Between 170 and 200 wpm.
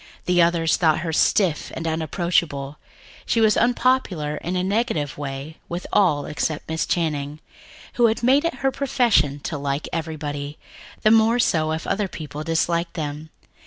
No: average, 155 wpm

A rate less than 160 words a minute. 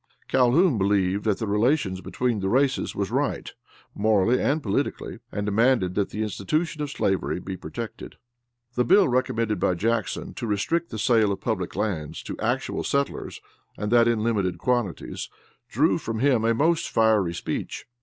No: average, 165 wpm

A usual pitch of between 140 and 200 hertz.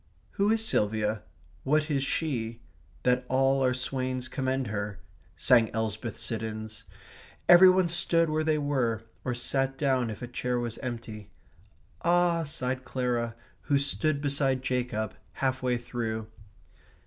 No: low, 130 Hz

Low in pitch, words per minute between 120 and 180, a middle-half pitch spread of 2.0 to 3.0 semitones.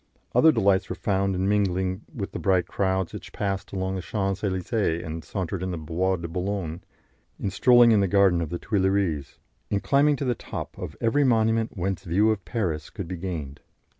No: very low, 95 Hz; average, 195 wpm; narrow, 2.6 semitones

